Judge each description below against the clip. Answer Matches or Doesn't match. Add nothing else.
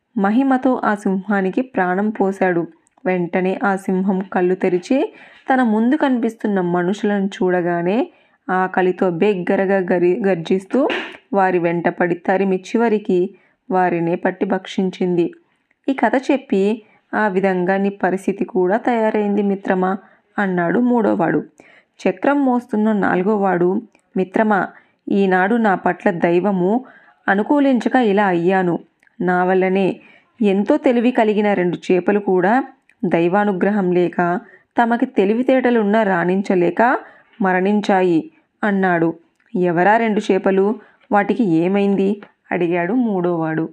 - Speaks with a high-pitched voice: Matches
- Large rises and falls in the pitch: Doesn't match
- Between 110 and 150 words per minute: Doesn't match